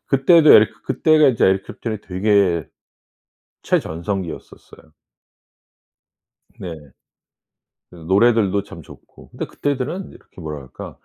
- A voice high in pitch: No, low, 100 Hz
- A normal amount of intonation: No, wide, 7.0 semitones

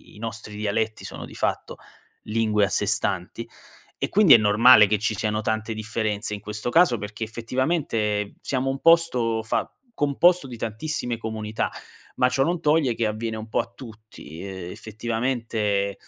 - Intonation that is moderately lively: Yes, average, 3.0 semitones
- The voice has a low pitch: Yes, low, 110 Hz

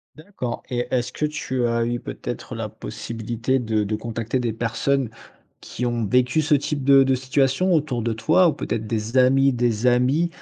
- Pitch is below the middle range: Yes, low, 125 Hz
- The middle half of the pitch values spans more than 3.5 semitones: No, average, 2.8 semitones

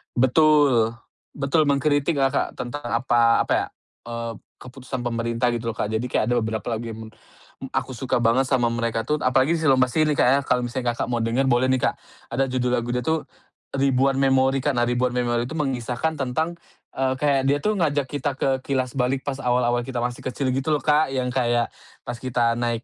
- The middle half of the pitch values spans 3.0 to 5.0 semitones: No, narrow, 2.4 semitones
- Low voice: Yes, low, 130 Hz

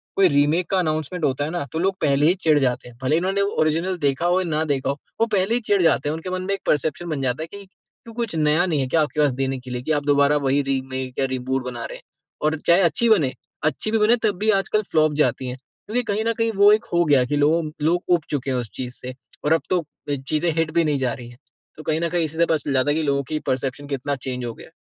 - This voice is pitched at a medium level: Yes, medium, 155 Hz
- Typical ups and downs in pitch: Yes, average, 4.7 semitones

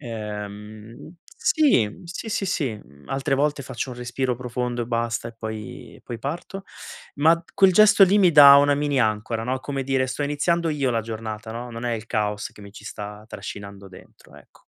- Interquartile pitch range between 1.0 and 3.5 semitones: No, average, 4.9 semitones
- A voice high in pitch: No, low, 125 Hz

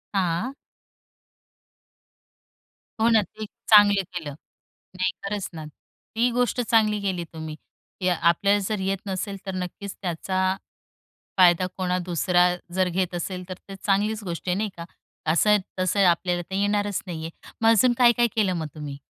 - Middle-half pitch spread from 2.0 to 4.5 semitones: Yes, average, 2.7 semitones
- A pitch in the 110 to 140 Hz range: No, high, 190 Hz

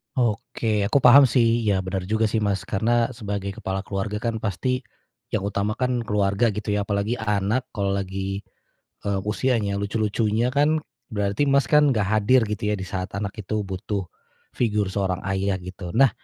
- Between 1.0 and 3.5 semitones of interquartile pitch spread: Yes, average, 2.9 semitones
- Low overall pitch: Yes, low, 105 Hz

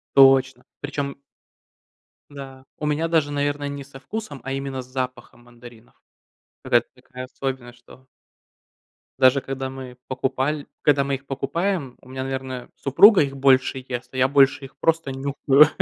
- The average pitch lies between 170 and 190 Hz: No, low, 135 Hz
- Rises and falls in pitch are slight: Yes, narrow, 1.6 semitones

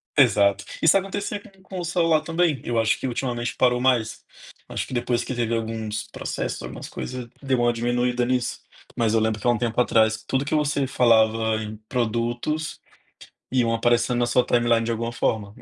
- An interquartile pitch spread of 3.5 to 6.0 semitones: No, narrow, 2.6 semitones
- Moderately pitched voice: No, low, 120 Hz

